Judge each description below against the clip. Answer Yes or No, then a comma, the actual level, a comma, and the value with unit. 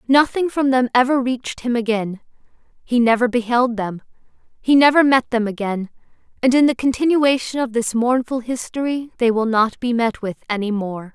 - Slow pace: No, average, 170 wpm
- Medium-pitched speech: No, high, 240 Hz